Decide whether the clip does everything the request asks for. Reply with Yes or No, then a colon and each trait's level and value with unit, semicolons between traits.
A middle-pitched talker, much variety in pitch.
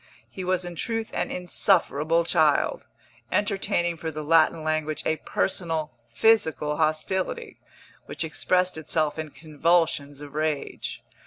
No: medium, 160 Hz; average, 2.8 semitones